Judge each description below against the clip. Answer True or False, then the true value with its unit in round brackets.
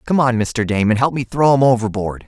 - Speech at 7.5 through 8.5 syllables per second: False (5.6 syllables/s)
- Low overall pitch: True (120 Hz)